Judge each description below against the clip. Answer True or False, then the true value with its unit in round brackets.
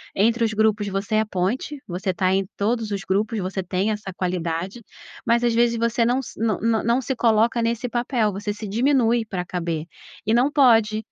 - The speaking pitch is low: False (220 Hz)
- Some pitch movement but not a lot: True (3.3 semitones)